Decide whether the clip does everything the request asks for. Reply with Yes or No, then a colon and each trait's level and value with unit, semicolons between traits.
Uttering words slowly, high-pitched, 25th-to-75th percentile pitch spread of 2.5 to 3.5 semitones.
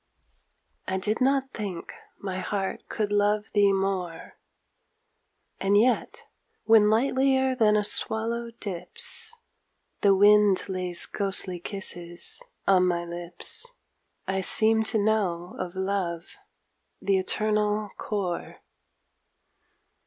Yes: slow, 105 wpm; high, 200 Hz; average, 2.8 semitones